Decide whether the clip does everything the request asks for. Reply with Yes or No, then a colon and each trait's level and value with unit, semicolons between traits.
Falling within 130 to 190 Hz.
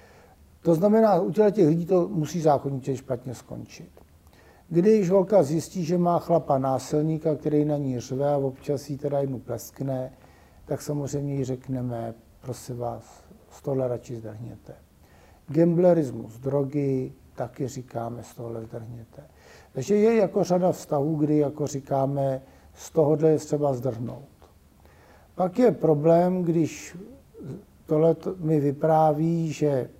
Yes: medium, 140 Hz